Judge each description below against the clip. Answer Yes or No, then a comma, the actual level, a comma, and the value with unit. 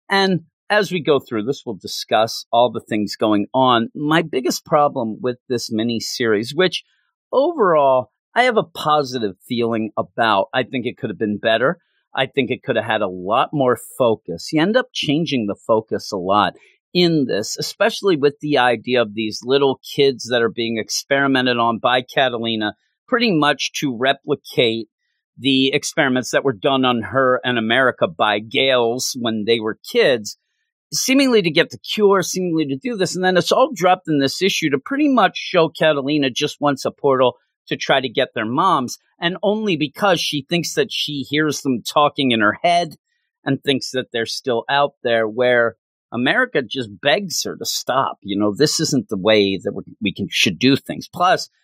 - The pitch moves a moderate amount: No, wide, 6.1 semitones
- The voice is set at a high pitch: No, low, 135 Hz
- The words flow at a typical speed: Yes, average, 185 wpm